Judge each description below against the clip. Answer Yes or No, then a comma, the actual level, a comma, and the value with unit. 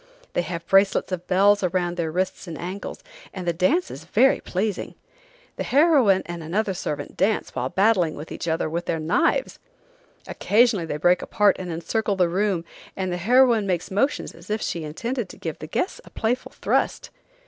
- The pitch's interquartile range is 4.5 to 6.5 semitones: No, average, 3.9 semitones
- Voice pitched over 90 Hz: Yes, medium, 185 Hz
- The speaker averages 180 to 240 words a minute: Yes, average, 185 wpm